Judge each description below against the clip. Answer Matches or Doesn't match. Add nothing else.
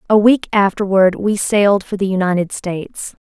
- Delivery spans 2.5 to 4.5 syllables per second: Doesn't match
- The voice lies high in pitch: Matches